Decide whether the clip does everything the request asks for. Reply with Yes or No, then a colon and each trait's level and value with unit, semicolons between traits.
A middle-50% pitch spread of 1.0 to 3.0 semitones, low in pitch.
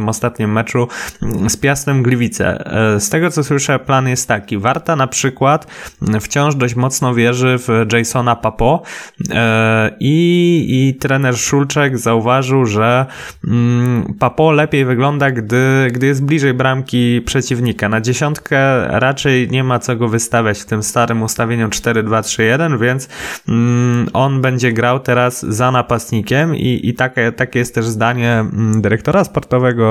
Yes: average, 2.7 semitones; low, 125 Hz